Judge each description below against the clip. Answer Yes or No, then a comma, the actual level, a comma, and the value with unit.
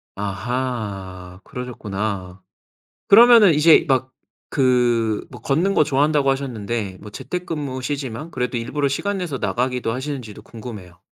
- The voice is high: No, low, 125 Hz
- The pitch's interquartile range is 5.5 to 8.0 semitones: No, average, 5.1 semitones